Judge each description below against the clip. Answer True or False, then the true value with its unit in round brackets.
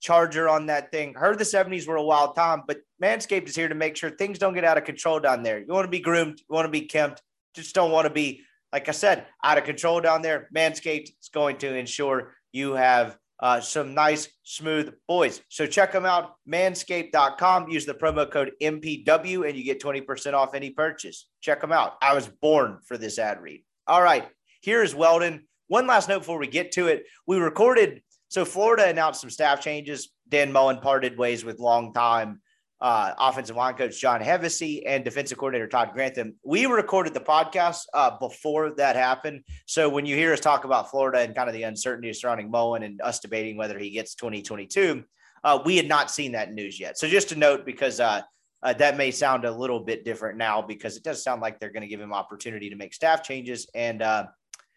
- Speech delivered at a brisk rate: True (215 wpm)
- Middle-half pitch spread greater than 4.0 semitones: True (4.4 semitones)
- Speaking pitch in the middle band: True (145 Hz)